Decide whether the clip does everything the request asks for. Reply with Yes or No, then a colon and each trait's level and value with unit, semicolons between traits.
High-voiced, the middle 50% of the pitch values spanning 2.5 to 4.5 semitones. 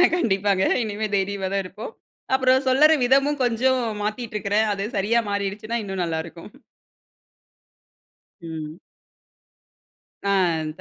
Yes: high, 205 Hz; average, 4.0 semitones